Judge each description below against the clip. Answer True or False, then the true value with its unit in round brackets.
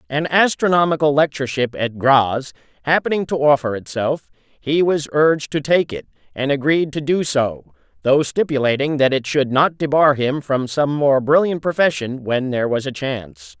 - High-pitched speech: False (140 Hz)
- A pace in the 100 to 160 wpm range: False (170 wpm)